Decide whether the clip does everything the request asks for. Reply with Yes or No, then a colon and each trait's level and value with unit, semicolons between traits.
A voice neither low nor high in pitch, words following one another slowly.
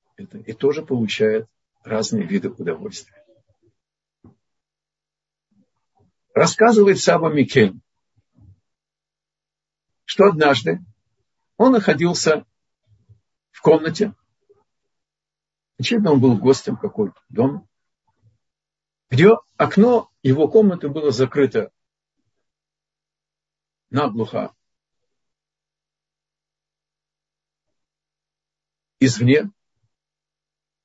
Yes: medium, 155 Hz; slow, 60 wpm